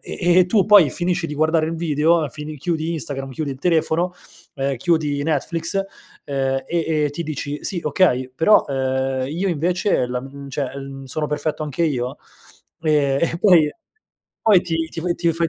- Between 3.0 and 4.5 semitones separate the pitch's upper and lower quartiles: Yes, average, 3.6 semitones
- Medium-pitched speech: Yes, medium, 155 Hz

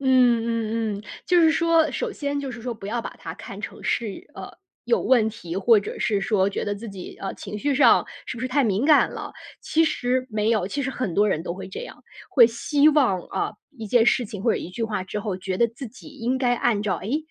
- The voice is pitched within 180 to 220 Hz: No, high, 230 Hz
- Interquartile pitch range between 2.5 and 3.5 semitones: No, average, 4.2 semitones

